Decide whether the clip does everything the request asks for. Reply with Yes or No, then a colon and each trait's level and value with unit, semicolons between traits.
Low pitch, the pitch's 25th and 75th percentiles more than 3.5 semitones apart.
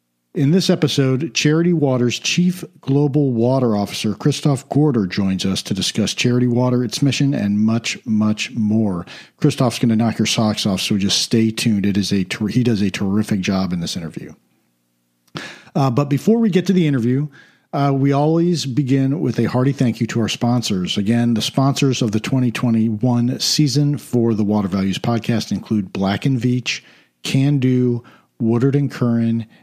Yes: low, 120 Hz; average, 4.5 semitones